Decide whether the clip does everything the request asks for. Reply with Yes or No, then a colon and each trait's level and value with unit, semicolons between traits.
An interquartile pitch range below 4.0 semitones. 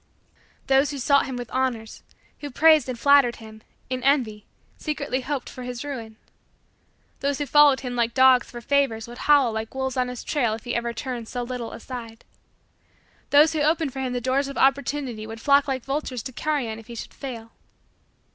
Yes: average, 3.0 semitones